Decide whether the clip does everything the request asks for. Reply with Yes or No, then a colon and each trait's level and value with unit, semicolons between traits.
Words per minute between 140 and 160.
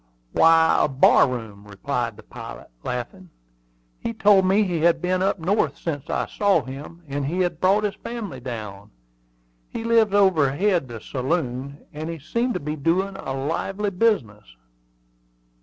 Yes: average, 155 wpm